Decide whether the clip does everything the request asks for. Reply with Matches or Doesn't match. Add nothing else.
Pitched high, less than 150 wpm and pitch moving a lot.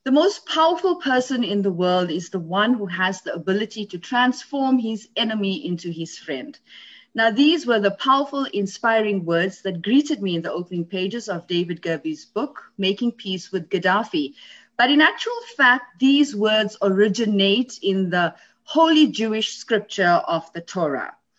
Doesn't match